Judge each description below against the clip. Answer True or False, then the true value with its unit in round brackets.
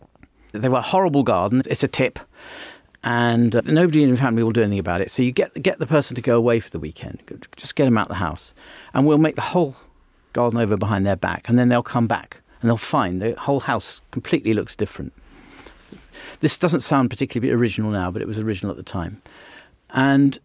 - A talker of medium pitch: False (120 Hz)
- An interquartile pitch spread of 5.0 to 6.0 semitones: False (4.1 semitones)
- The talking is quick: True (220 wpm)